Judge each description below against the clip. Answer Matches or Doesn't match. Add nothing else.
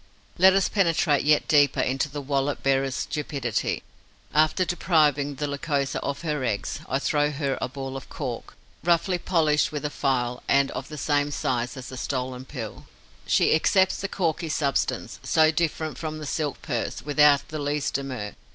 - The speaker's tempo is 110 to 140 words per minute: Doesn't match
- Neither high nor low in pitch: Matches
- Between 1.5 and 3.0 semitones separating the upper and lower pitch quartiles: Matches